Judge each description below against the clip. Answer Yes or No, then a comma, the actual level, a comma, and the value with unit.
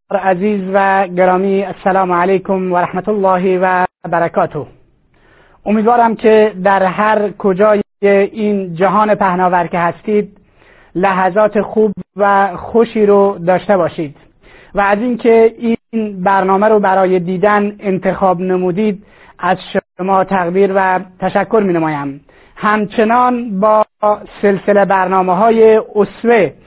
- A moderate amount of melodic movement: No, narrow, 2.2 semitones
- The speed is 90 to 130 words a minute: Yes, average, 110 wpm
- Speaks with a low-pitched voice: No, high, 195 Hz